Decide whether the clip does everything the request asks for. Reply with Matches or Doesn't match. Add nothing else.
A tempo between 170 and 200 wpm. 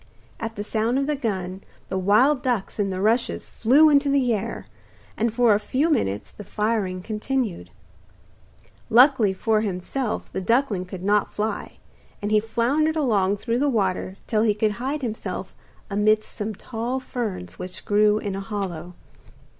Doesn't match